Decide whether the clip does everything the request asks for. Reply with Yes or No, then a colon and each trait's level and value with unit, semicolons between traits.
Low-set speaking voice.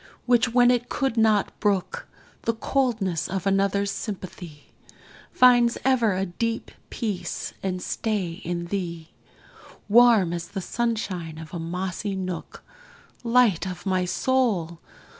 No: high, 195 Hz